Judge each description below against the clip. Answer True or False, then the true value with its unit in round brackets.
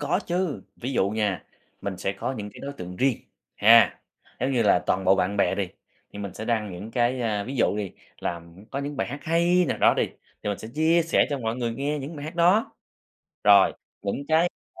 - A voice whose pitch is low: True (120 Hz)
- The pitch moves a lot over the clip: True (6.2 semitones)